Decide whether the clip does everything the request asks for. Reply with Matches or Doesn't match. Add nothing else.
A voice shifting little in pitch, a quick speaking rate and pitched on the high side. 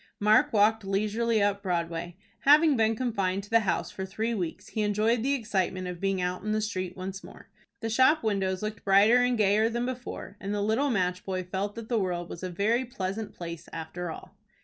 Doesn't match